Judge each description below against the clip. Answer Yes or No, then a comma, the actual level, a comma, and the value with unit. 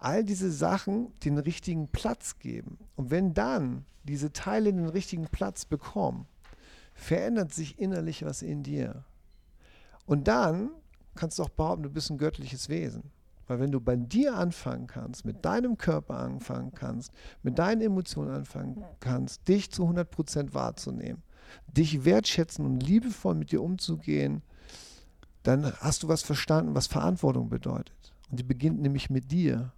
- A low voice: No, medium, 150 Hz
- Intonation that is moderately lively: No, wide, 7.5 semitones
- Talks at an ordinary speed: Yes, average, 155 wpm